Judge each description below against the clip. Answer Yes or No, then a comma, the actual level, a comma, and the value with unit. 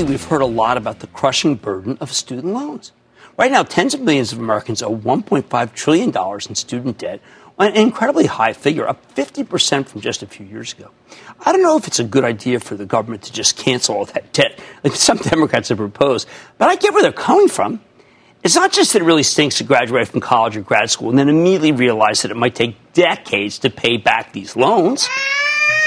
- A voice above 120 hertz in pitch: Yes, medium, 140 Hz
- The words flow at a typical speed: No, fast, 215 wpm